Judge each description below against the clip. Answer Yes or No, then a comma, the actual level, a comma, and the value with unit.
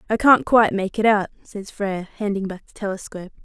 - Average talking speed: No, fast, 210 wpm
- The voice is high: Yes, high, 205 Hz